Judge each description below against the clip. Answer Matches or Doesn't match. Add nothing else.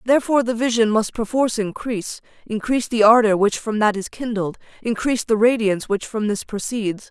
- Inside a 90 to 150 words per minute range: Doesn't match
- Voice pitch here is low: Doesn't match